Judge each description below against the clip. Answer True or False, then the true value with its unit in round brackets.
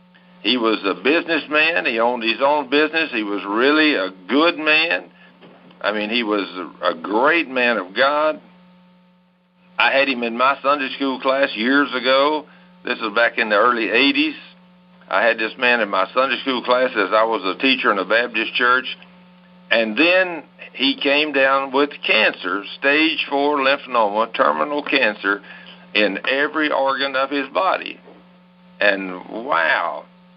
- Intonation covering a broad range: True (6.5 semitones)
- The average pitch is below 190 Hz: True (140 Hz)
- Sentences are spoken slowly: False (155 wpm)